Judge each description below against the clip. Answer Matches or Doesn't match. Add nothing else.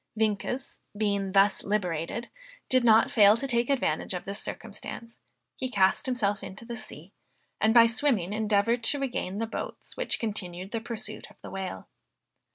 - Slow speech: Doesn't match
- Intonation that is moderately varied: Matches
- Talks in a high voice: Matches